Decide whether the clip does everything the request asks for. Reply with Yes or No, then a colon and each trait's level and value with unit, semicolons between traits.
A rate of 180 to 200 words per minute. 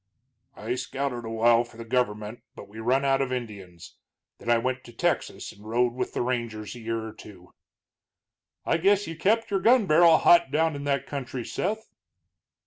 Yes: average, 190 wpm